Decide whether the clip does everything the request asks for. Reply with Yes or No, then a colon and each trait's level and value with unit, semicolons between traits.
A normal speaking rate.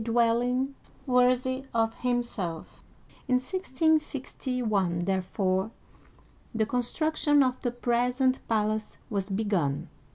No: slow, 95 wpm